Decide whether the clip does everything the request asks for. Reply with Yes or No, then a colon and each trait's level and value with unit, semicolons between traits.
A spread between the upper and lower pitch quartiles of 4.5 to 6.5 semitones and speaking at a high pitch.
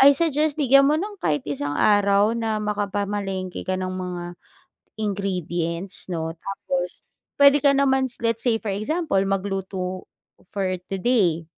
Yes: average, 5.3 semitones; high, 200 Hz